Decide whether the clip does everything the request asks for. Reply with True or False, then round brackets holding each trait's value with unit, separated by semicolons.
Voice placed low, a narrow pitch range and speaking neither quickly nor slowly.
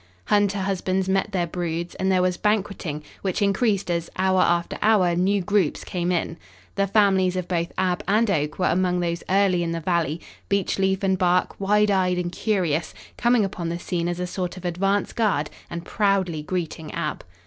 False (185 Hz; 2.3 semitones; 185 wpm)